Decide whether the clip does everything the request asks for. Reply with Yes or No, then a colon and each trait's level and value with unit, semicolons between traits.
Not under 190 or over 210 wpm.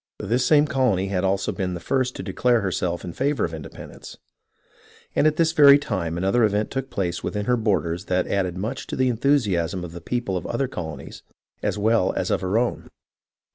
Yes: fast, 205 wpm